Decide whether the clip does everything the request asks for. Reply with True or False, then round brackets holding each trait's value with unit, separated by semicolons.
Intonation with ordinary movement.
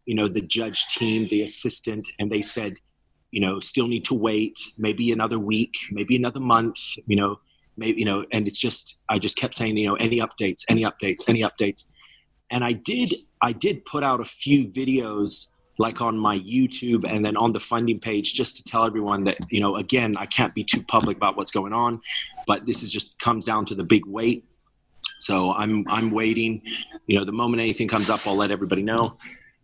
False (1.9 semitones)